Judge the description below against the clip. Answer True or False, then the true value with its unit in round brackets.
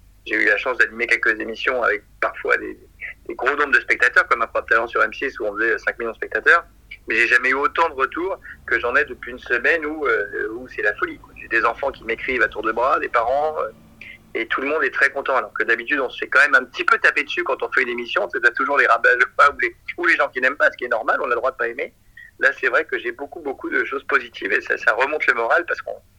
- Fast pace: True (285 wpm)